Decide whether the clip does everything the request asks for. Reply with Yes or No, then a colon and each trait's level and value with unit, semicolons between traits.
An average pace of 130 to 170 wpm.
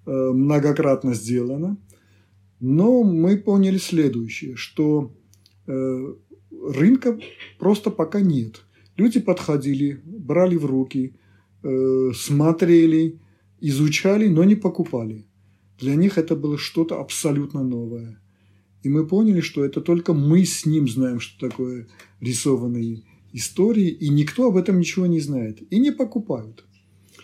No: average, 115 wpm